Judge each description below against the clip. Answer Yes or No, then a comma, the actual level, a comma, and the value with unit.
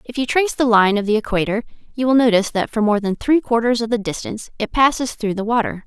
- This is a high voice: Yes, high, 225 Hz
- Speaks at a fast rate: Yes, fast, 255 wpm